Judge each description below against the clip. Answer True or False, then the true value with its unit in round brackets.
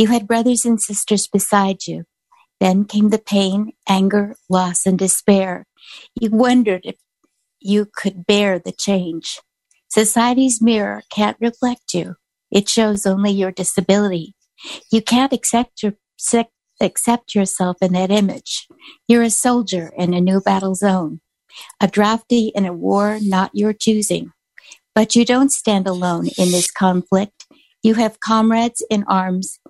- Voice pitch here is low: False (205 Hz)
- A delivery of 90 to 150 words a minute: True (140 wpm)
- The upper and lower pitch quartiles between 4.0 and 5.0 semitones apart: False (3.4 semitones)